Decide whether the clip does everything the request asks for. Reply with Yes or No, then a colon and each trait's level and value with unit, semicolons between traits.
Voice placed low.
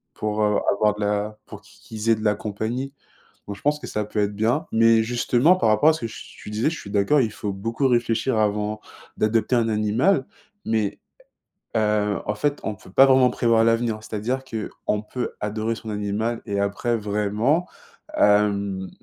Yes: low, 110 Hz